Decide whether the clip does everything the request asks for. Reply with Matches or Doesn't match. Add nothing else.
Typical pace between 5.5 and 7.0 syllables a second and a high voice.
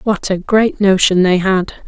Doesn't match